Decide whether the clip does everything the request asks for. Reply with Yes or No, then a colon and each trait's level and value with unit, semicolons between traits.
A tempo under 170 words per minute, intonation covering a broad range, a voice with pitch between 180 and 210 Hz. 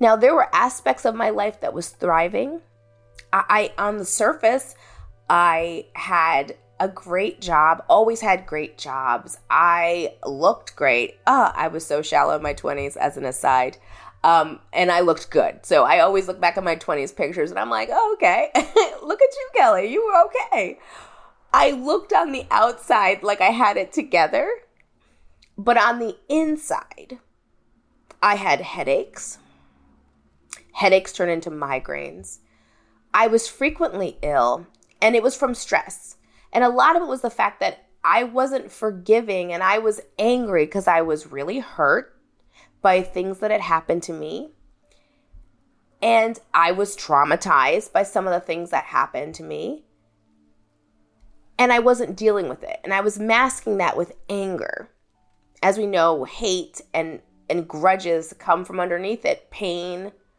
Yes: average, 160 wpm; wide, 6.8 semitones; medium, 185 Hz